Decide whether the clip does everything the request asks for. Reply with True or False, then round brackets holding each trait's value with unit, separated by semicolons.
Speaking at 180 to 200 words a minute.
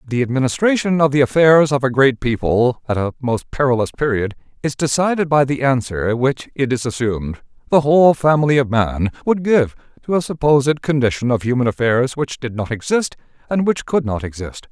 True (190 wpm)